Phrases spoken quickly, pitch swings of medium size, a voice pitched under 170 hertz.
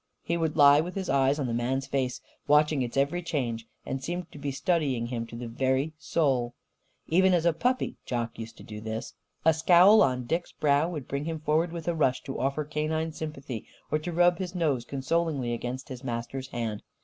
Yes: fast, 210 wpm; average, 4.5 semitones; medium, 140 Hz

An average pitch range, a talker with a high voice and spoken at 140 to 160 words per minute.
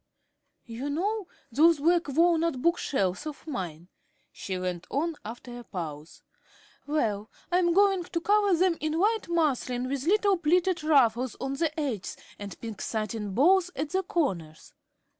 No: wide, 7.3 semitones; very high, 295 Hz; average, 155 wpm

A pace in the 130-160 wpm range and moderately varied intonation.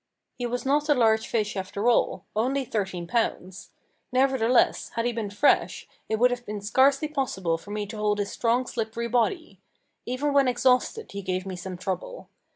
No: average, 180 wpm; average, 4.1 semitones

